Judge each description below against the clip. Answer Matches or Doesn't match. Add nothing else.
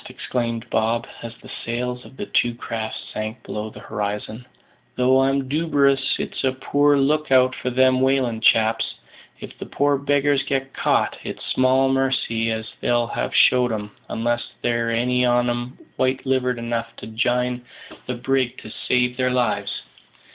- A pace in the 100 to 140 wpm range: Doesn't match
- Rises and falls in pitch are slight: Matches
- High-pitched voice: Doesn't match